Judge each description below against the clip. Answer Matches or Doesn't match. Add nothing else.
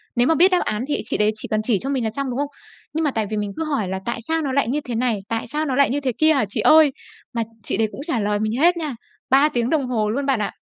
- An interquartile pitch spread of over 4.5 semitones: Matches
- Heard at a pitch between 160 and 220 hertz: Doesn't match